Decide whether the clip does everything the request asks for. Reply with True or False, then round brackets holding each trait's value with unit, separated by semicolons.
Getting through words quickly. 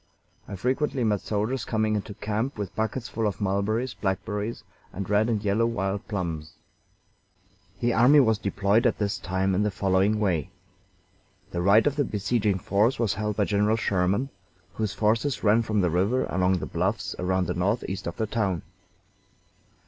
False (170 wpm)